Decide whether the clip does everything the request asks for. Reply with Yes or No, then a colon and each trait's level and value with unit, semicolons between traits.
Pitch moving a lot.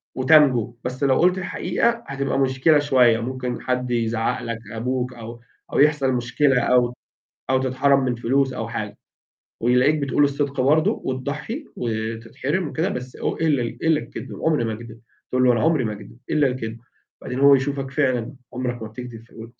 No: average, 3.1 semitones